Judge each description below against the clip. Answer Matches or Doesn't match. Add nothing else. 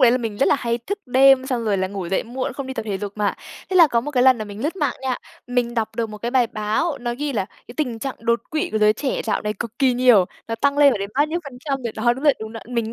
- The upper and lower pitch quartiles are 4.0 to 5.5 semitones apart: Doesn't match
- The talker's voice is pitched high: Matches